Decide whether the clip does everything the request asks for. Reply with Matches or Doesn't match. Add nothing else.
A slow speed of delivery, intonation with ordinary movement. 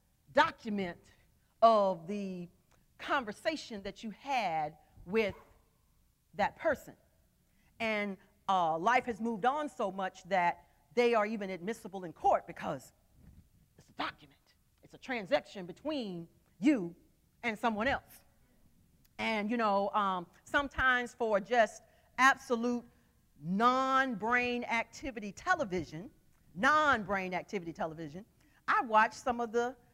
Matches